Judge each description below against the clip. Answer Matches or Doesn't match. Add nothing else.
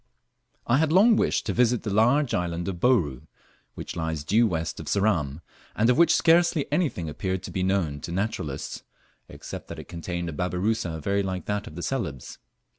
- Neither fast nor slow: Matches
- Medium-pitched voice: Doesn't match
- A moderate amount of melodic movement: Doesn't match